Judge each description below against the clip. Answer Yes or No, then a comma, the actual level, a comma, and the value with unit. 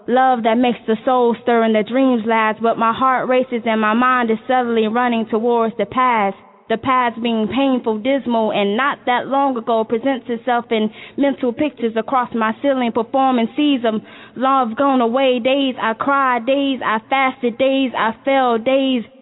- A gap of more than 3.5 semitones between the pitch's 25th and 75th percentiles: No, average, 2.7 semitones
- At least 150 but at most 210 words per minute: Yes, average, 175 wpm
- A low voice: No, high, 245 Hz